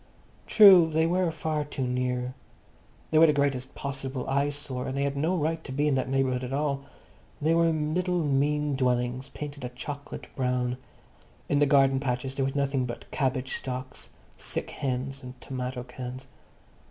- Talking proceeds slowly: No, average, 170 wpm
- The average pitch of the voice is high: No, low, 135 Hz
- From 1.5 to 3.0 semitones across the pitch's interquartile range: Yes, narrow, 2.6 semitones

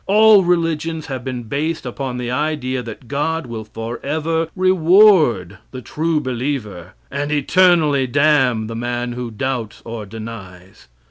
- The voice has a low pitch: Yes, low, 130 Hz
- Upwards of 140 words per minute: No, slow, 135 wpm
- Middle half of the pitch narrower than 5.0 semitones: No, average, 5.3 semitones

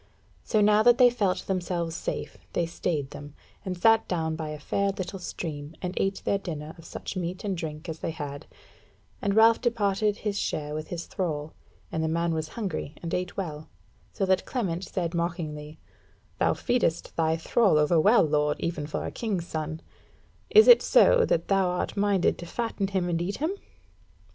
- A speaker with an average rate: Yes, average, 185 wpm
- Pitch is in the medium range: Yes, medium, 175 Hz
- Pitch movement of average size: Yes, average, 4.0 semitones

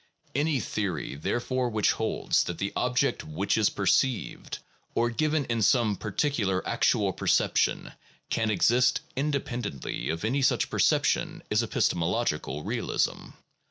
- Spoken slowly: Yes, slow, 125 wpm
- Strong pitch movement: No, average, 4.7 semitones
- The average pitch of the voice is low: Yes, low, 115 Hz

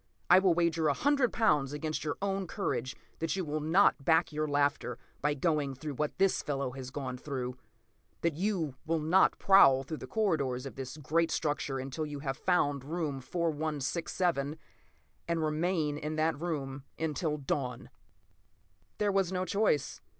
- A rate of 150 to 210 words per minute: Yes, average, 160 wpm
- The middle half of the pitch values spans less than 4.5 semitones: Yes, average, 3.6 semitones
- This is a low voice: No, medium, 155 Hz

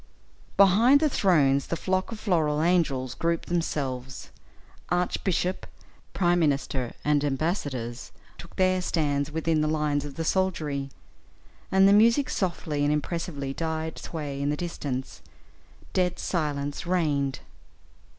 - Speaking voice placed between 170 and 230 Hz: No, medium, 160 Hz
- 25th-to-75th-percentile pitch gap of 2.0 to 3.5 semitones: No, average, 4.0 semitones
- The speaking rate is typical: No, slow, 125 wpm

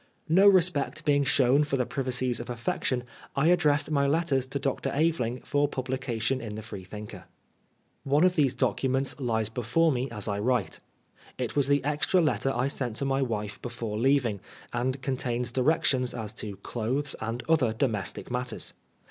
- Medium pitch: No, low, 130 Hz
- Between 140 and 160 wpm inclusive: No, average, 170 wpm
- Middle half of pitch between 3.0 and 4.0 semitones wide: Yes, average, 3.3 semitones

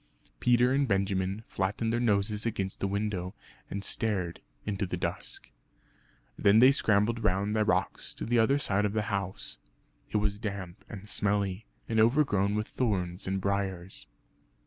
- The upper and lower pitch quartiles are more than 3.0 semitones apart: No, narrow, 2.4 semitones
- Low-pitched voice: Yes, low, 100 Hz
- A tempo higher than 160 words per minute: No, average, 155 wpm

